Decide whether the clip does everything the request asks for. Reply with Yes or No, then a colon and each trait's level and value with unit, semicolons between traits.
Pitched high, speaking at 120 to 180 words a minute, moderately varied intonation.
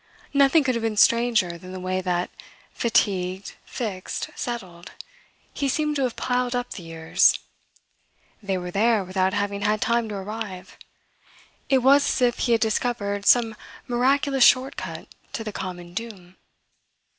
Yes: high, 215 Hz; average, 155 wpm; average, 4.7 semitones